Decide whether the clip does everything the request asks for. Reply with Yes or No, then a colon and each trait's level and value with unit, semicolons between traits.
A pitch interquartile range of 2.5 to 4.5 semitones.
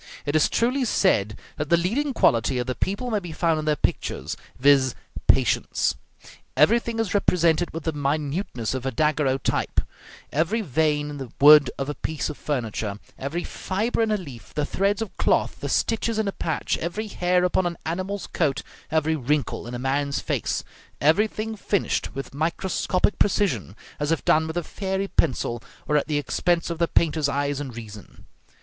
No: average, 5.2 semitones